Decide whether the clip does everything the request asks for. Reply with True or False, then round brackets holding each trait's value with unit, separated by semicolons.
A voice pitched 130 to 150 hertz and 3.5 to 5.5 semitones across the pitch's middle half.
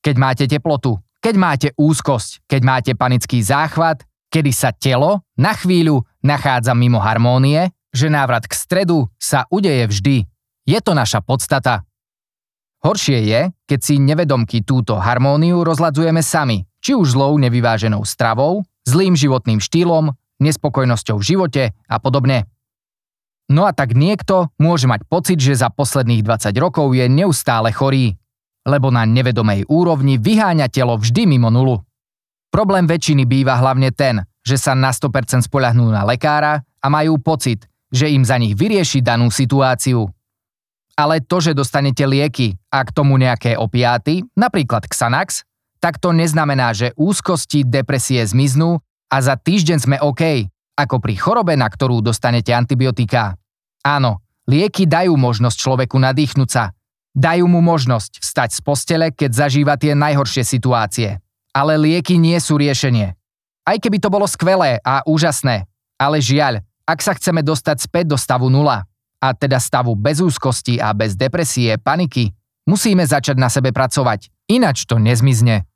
True (135 Hz; 4.3 semitones)